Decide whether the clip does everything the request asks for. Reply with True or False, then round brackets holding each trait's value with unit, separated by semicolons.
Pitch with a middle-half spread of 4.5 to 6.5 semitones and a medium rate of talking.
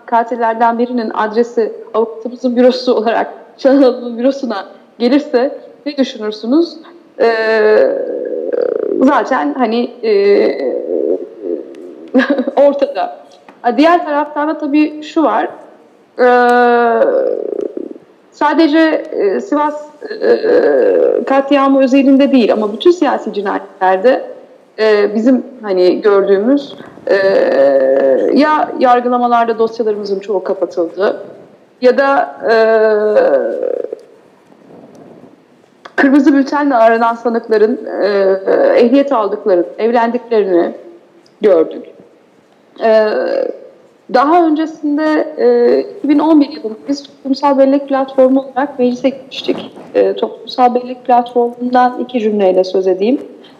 False (5.6 semitones; 80 wpm)